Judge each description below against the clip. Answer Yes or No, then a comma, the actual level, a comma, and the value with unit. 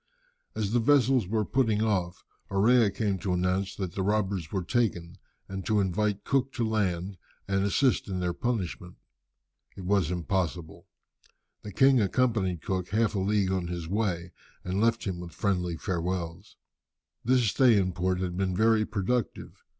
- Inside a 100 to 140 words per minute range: No, average, 160 wpm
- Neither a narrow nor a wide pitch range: Yes, average, 3.4 semitones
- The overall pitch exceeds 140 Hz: No, very low, 95 Hz